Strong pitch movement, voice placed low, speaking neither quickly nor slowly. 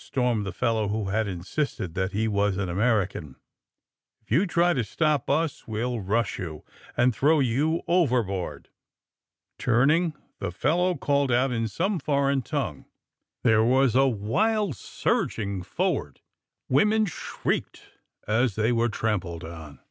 Yes: wide, 6.1 semitones; low, 120 Hz; average, 145 wpm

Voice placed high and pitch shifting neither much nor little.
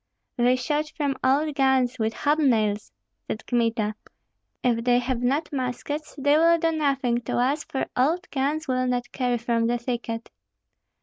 Yes: very high, 255 Hz; average, 3.3 semitones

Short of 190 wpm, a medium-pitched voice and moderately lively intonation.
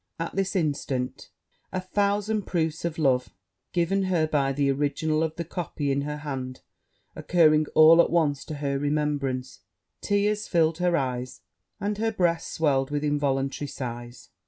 Yes: average, 155 wpm; medium, 155 Hz; average, 3.8 semitones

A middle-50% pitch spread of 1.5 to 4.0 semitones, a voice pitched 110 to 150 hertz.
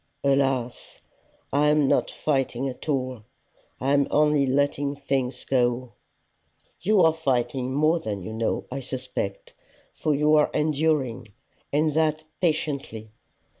Yes: average, 3.0 semitones; medium, 140 Hz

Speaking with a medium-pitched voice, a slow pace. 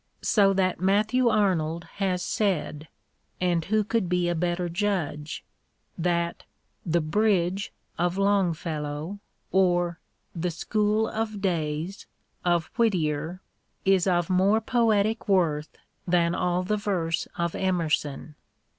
Yes: medium, 180 Hz; slow, 130 wpm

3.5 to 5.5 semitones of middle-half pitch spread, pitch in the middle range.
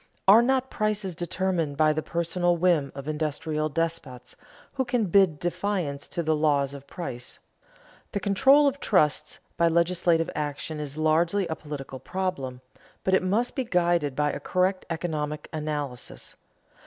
Yes: average, 3.9 semitones; medium, 165 Hz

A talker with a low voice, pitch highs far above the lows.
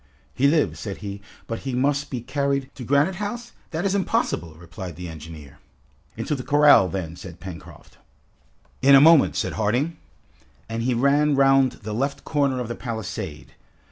Yes: low, 130 Hz; wide, 6.4 semitones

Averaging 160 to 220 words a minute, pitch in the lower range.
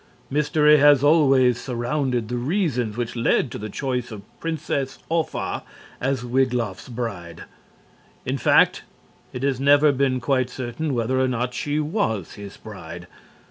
No: average, 140 wpm; low, 130 Hz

